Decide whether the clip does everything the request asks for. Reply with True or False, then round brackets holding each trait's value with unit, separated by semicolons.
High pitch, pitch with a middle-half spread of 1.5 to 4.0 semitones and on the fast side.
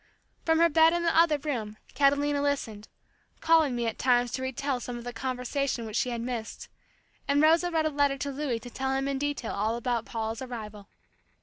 True (265 Hz; 3.6 semitones; 210 wpm)